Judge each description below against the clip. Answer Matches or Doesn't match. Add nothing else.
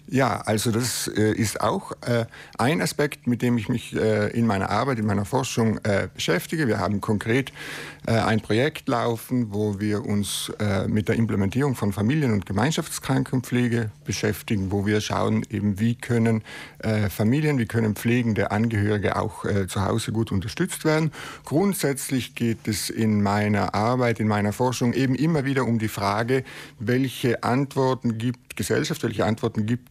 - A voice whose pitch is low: Matches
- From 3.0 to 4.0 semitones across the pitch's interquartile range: Matches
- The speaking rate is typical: Matches